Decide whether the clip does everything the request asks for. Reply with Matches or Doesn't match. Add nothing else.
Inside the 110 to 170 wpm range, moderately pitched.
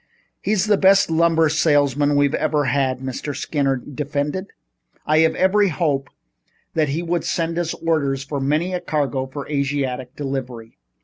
Matches